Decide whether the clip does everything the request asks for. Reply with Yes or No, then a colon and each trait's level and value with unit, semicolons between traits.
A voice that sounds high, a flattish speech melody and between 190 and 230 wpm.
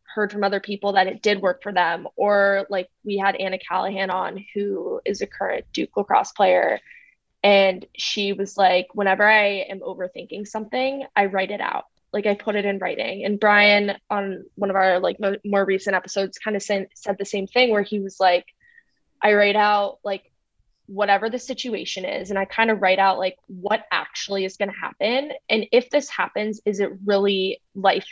Yes: high, 200 Hz; narrow, 1.5 semitones; average, 200 wpm